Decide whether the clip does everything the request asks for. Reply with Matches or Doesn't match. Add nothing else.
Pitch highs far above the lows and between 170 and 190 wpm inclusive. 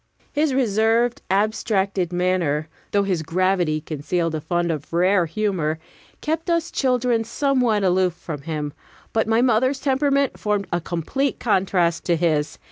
Doesn't match